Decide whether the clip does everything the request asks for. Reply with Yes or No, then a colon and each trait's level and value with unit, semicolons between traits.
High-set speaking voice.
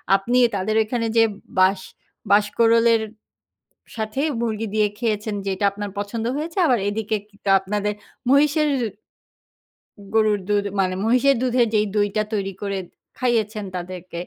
Yes: high, 215 Hz